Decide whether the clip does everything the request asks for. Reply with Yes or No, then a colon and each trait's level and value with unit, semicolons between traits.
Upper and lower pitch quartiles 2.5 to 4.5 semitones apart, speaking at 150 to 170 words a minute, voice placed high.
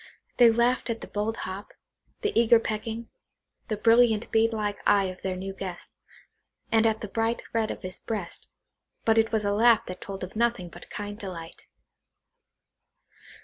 Yes: average, 2.8 semitones; average, 155 wpm; high, 215 Hz